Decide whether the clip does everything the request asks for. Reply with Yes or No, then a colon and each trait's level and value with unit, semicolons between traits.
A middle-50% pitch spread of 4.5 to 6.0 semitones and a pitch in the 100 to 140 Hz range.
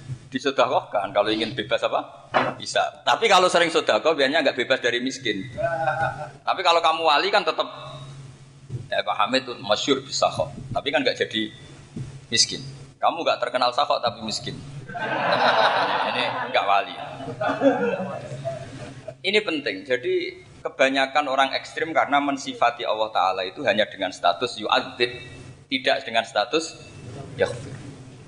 No: average, 3.7 semitones; low, 135 Hz